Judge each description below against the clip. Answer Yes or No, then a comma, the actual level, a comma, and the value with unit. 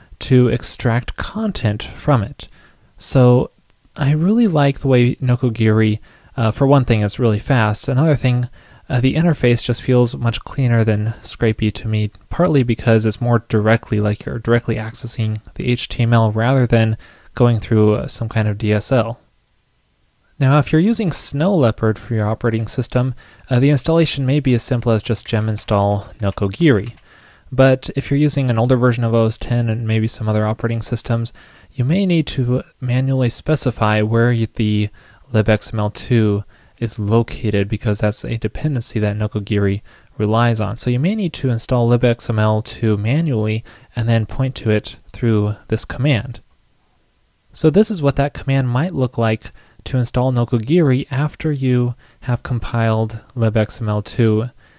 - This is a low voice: Yes, low, 115 Hz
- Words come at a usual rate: Yes, average, 155 wpm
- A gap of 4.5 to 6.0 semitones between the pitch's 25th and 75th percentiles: No, average, 3.1 semitones